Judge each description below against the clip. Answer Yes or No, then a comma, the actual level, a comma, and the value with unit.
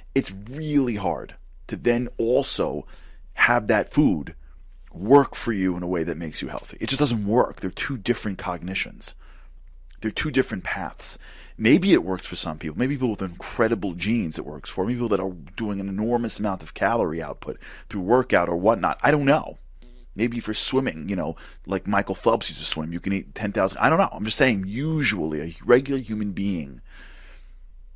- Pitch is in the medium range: No, low, 100 Hz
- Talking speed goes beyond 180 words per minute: Yes, average, 195 wpm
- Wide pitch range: Yes, wide, 6.2 semitones